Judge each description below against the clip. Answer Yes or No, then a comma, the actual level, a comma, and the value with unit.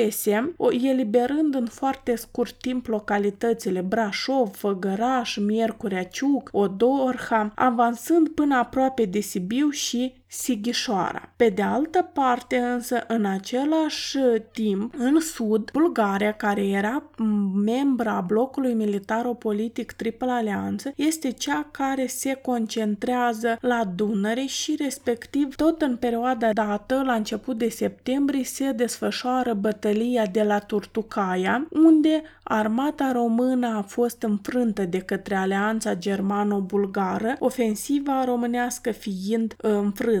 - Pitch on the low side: No, high, 235 Hz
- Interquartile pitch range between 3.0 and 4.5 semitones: Yes, average, 3.5 semitones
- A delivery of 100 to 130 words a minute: Yes, slow, 115 wpm